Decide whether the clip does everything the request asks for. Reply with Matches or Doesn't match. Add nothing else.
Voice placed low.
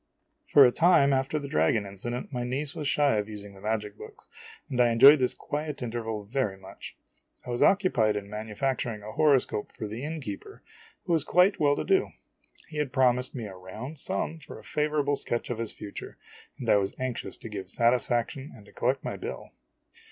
Matches